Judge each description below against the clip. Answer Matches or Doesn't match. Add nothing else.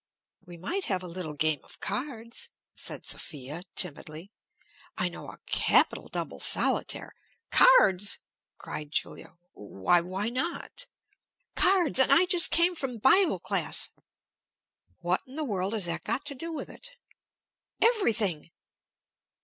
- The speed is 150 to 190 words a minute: Doesn't match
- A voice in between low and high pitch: Doesn't match